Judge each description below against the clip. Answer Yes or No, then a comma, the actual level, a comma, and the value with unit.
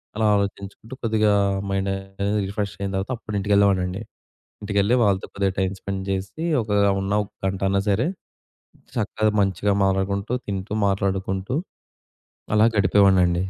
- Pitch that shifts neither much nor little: No, narrow, 1.2 semitones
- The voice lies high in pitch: No, low, 100 Hz